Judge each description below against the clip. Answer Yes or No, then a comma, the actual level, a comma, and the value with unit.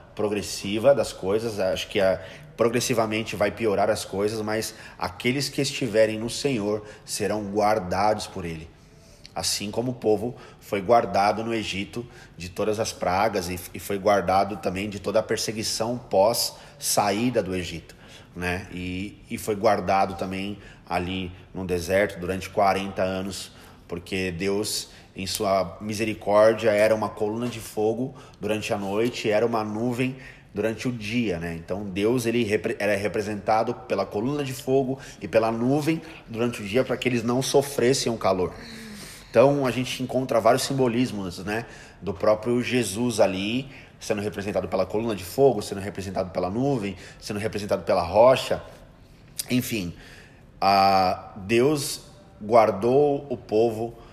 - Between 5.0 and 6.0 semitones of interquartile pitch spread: No, average, 4.0 semitones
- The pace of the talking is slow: No, average, 145 wpm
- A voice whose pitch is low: Yes, low, 110 Hz